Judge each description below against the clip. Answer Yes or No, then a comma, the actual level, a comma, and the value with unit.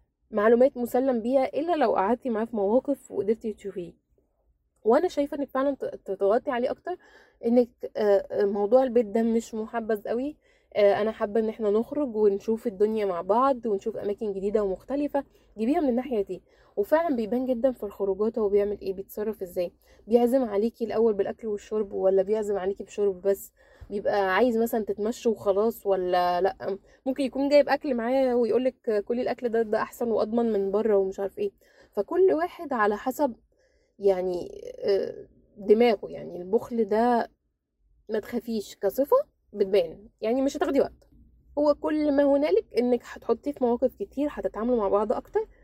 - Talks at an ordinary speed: No, fast, 155 wpm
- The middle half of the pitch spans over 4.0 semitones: Yes, average, 4.8 semitones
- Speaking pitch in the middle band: No, high, 230 Hz